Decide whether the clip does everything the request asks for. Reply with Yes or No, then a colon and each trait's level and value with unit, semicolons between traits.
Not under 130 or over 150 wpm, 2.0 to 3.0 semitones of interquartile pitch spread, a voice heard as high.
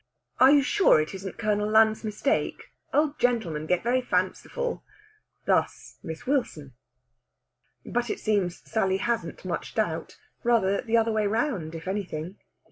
No: average, 140 wpm; average, 4.6 semitones; high, 215 Hz